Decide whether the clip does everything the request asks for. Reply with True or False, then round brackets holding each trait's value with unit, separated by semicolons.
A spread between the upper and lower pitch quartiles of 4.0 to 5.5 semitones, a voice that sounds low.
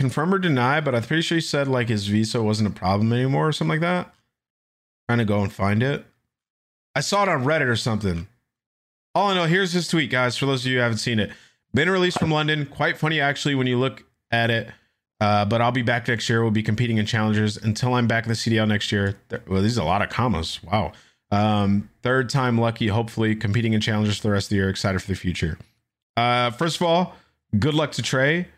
True (4.4 semitones; 115 Hz)